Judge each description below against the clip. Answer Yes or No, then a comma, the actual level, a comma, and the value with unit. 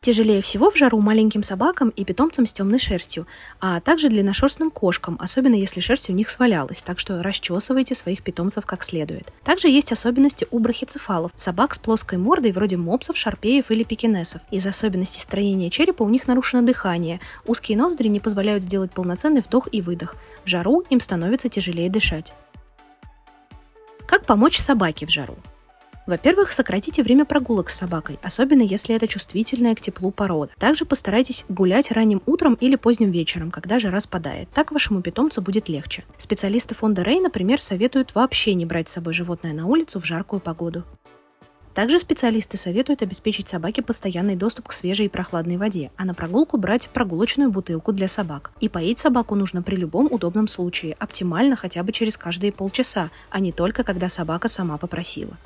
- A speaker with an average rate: No, fast, 170 wpm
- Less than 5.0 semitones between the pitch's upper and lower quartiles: No, wide, 5.6 semitones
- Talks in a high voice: Yes, high, 210 Hz